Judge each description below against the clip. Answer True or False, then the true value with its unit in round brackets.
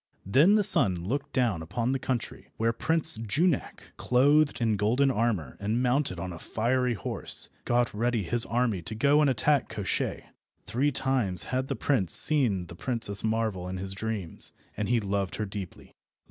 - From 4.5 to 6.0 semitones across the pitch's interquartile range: True (4.9 semitones)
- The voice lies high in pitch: False (115 Hz)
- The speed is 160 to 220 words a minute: True (175 wpm)